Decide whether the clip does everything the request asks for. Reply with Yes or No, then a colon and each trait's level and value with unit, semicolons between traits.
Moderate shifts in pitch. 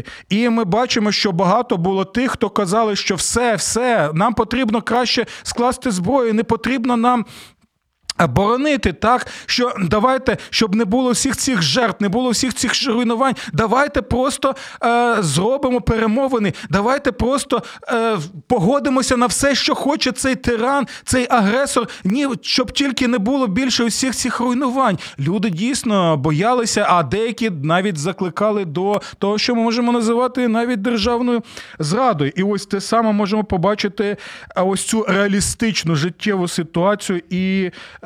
Yes: average, 3.7 semitones